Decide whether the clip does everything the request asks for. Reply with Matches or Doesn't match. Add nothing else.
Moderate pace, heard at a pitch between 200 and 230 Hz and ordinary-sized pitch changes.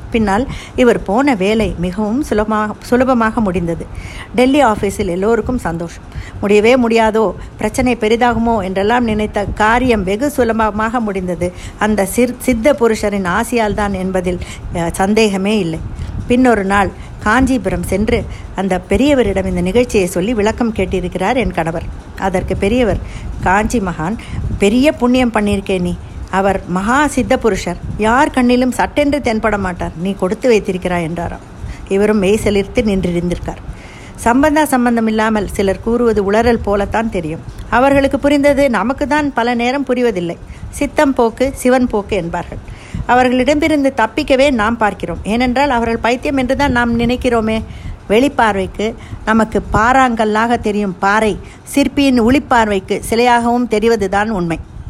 Matches